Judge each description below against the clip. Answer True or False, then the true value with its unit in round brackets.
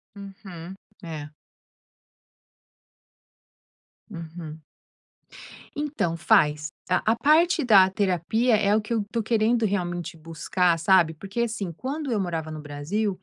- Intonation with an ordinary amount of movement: True (5.0 semitones)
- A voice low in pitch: False (190 Hz)